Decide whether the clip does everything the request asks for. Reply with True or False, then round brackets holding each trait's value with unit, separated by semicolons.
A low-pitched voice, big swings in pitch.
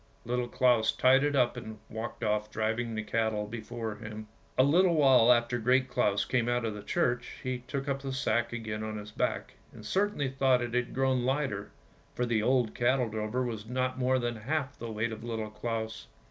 False (120 Hz; 2.8 semitones)